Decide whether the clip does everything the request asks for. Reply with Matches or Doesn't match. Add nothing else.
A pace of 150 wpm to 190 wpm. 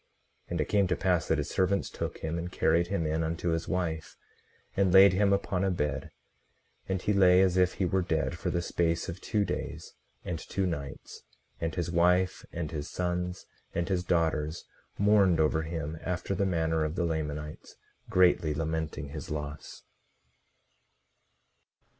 Matches